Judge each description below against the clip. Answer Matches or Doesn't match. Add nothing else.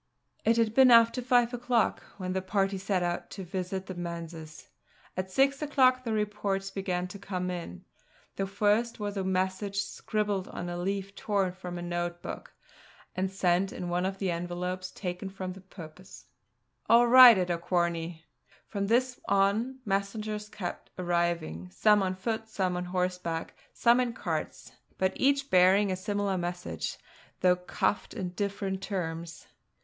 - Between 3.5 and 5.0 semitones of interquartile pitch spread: Doesn't match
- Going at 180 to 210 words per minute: Doesn't match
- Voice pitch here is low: Doesn't match